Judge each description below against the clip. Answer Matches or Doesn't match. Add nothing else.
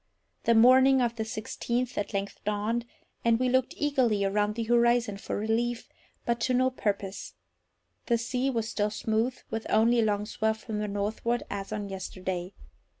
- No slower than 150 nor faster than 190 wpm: Matches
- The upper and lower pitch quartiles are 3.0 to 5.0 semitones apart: Doesn't match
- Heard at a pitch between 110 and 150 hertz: Doesn't match